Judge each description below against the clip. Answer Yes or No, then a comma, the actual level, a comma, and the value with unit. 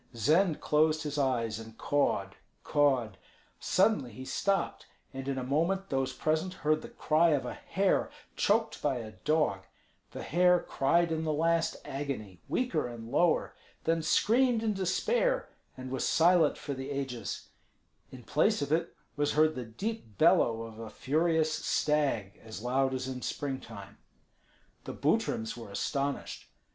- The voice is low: No, medium, 145 Hz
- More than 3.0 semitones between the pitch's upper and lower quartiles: Yes, average, 5.1 semitones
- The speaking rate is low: No, average, 155 wpm